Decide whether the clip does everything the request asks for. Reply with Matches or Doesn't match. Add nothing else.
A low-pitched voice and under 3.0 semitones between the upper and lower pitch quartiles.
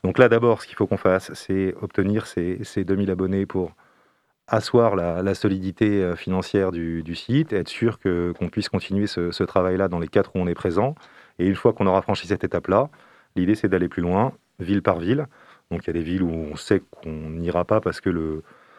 Matches